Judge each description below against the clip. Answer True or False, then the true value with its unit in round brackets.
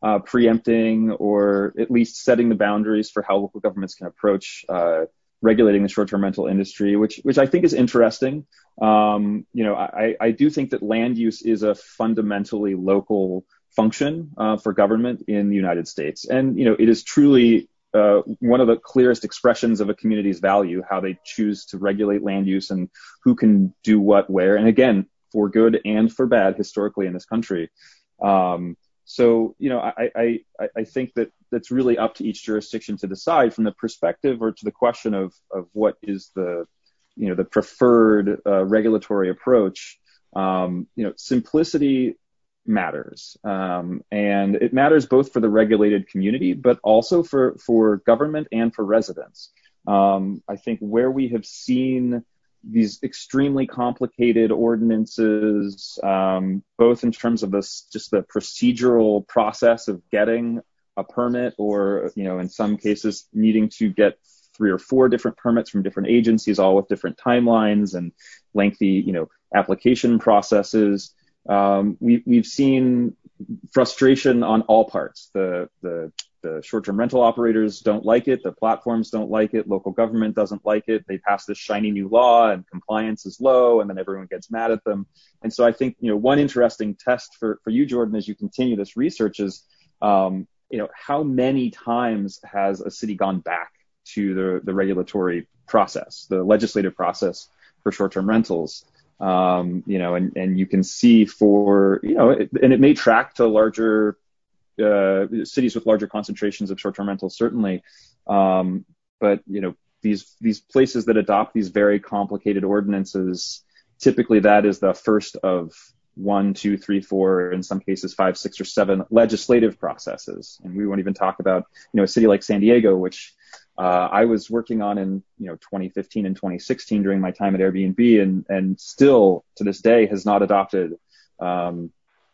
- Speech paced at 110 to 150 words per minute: False (175 wpm)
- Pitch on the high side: False (105 Hz)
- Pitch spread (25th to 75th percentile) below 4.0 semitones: True (3.0 semitones)